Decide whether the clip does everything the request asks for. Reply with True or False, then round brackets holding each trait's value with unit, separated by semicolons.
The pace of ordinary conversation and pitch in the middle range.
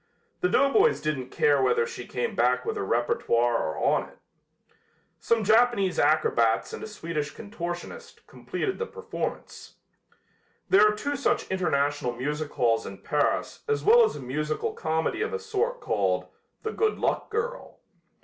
True (155 wpm; 170 Hz)